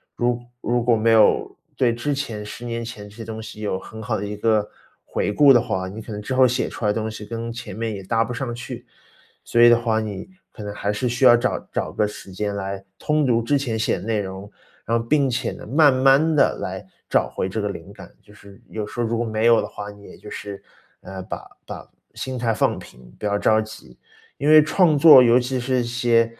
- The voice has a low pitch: Yes, low, 115 Hz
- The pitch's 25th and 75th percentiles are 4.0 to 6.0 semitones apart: No, average, 2.9 semitones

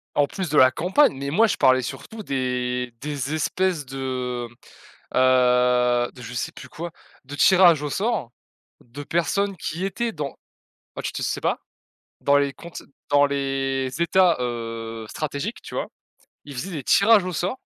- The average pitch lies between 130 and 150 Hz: Yes, medium, 140 Hz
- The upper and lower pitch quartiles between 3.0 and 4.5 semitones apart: No, wide, 5.6 semitones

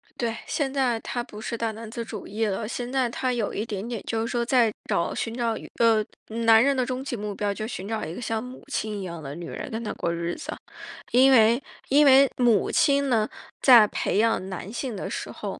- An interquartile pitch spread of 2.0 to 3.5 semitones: Yes, average, 2.8 semitones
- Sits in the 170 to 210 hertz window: No, high, 230 Hz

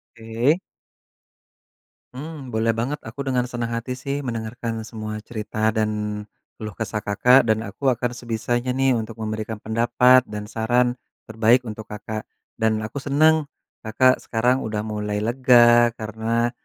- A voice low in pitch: Yes, low, 115 Hz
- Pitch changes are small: Yes, narrow, 2.3 semitones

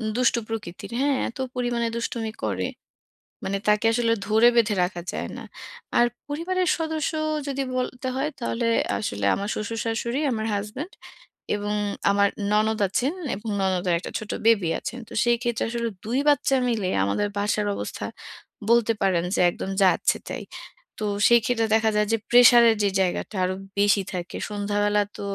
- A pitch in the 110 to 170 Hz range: No, high, 220 Hz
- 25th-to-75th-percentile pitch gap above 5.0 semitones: No, average, 2.9 semitones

